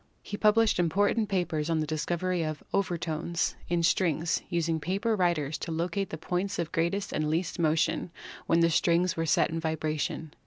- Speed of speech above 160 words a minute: Yes, average, 170 wpm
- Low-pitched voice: No, medium, 170 Hz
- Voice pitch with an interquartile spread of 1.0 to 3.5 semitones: Yes, narrow, 2.4 semitones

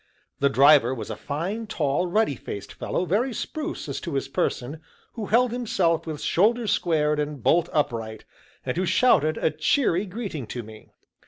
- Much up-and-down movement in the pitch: Yes, wide, 6.9 semitones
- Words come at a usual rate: Yes, average, 170 wpm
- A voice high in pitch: No, medium, 165 Hz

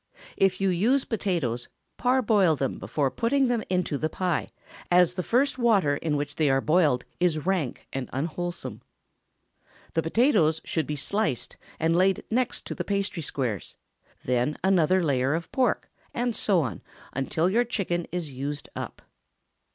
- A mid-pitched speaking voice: Yes, medium, 175 Hz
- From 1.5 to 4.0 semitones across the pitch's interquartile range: No, wide, 5.4 semitones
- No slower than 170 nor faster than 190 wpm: No, average, 150 wpm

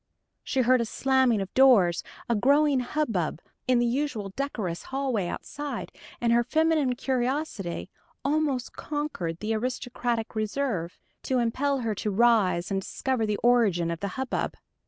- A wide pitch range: No, average, 4.3 semitones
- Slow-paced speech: No, average, 145 wpm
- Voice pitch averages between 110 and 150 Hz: No, high, 240 Hz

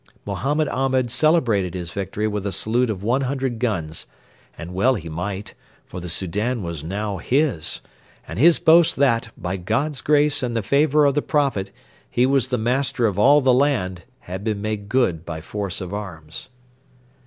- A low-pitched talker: Yes, low, 110 Hz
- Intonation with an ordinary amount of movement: No, wide, 6.2 semitones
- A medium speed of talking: Yes, average, 175 wpm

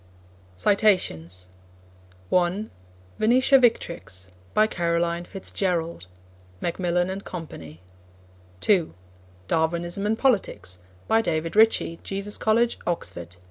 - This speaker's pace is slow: Yes, slow, 90 wpm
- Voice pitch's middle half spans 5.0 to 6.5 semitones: No, average, 4.3 semitones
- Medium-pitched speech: Yes, medium, 180 Hz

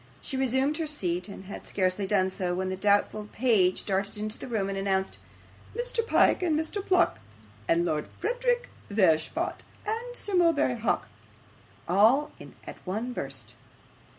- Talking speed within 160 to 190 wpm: No, average, 150 wpm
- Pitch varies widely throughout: Yes, wide, 9.0 semitones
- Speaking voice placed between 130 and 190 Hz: No, high, 215 Hz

